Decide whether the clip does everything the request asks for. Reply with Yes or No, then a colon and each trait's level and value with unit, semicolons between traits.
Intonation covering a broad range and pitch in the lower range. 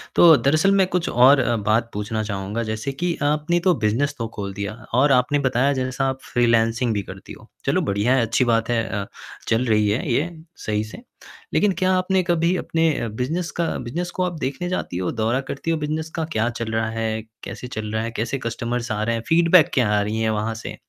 Yes: wide, 5.9 semitones; low, 120 Hz